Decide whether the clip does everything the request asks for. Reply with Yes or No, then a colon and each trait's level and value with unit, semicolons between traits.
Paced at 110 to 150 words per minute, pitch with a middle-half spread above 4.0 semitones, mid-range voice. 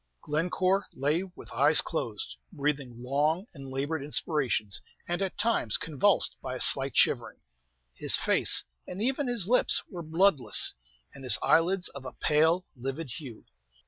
Yes: average, 145 wpm; average, 5.2 semitones; medium, 155 Hz